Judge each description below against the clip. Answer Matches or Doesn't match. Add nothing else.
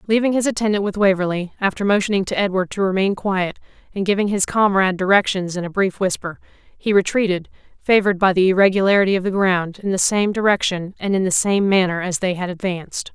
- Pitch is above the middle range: Matches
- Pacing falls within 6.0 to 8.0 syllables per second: Matches